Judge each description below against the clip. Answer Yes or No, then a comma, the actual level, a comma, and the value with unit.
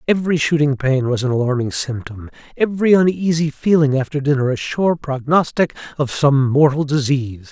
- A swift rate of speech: No, average, 145 wpm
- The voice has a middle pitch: Yes, medium, 145 Hz